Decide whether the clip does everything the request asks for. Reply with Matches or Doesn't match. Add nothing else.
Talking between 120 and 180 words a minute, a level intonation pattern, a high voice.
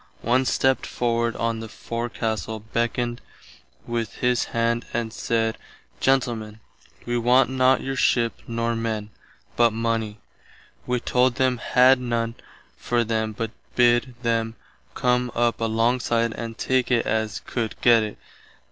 Doesn't match